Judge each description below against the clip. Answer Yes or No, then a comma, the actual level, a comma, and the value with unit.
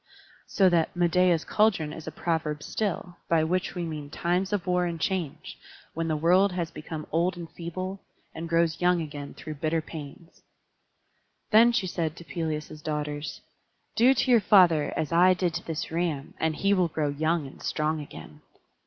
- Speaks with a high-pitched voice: No, medium, 165 Hz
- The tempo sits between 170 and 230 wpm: Yes, average, 180 wpm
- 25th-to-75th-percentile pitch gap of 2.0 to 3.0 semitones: Yes, average, 2.7 semitones